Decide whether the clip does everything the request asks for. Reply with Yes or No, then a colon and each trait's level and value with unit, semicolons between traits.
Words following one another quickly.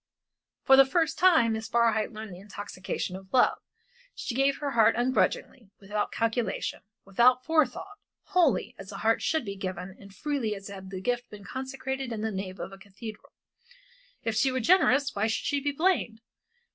No: average, 180 wpm